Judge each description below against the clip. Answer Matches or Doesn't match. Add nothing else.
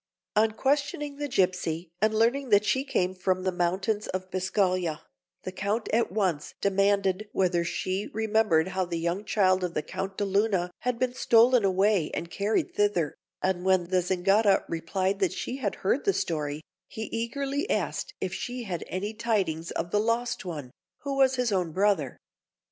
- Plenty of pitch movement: Doesn't match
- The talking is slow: Doesn't match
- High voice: Matches